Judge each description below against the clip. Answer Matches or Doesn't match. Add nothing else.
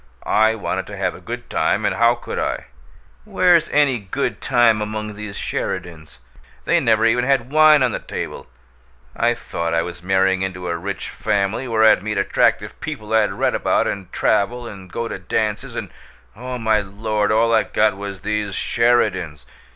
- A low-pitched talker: Matches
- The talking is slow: Doesn't match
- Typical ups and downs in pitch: Matches